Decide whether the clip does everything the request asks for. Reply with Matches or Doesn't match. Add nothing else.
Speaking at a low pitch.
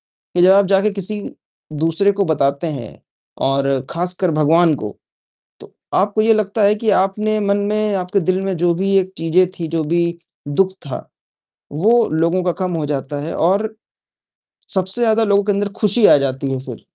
Doesn't match